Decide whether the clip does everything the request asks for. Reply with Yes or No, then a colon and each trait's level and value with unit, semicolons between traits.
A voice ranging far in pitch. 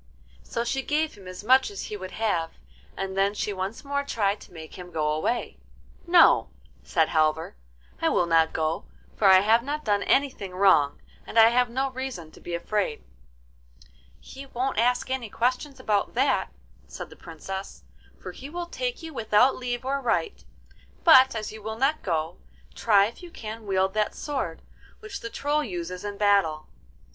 Yes: wide, 6.2 semitones